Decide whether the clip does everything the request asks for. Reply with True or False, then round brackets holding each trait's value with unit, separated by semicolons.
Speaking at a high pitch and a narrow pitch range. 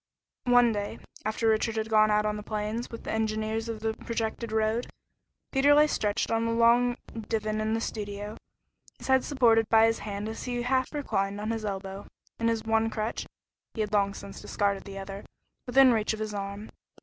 True (220 Hz; 1.6 semitones)